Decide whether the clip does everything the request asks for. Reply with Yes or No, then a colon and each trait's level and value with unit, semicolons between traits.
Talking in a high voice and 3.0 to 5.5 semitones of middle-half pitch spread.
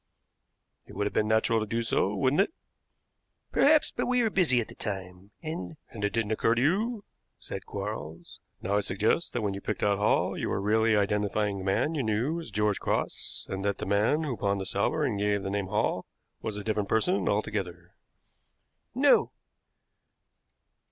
No: low, 105 Hz; average, 4.0 semitones